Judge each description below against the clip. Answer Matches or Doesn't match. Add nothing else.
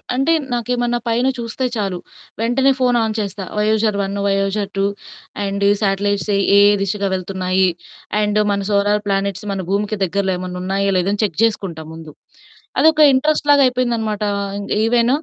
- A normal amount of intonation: Matches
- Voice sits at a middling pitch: Doesn't match